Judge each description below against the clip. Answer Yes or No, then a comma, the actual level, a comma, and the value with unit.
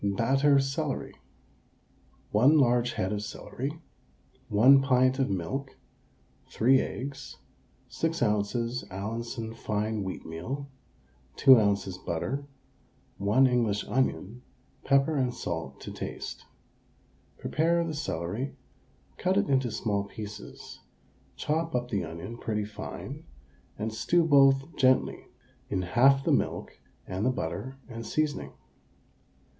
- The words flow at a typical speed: No, slow, 115 wpm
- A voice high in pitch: No, low, 120 Hz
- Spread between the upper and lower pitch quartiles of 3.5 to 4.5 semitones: No, average, 4.9 semitones